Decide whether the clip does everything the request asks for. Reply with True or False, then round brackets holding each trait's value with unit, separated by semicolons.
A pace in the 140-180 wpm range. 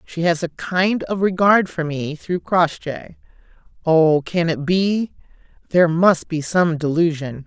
True (145 wpm)